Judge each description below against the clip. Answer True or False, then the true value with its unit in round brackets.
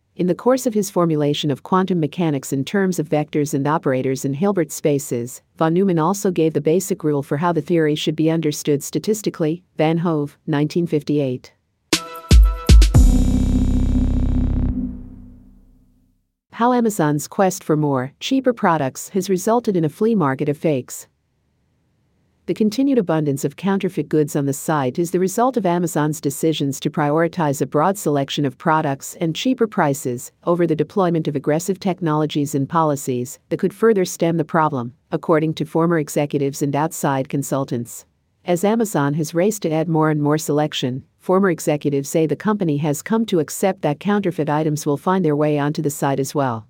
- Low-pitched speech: False (155 Hz)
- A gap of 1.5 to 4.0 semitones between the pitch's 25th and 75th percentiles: True (3.5 semitones)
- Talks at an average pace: True (165 wpm)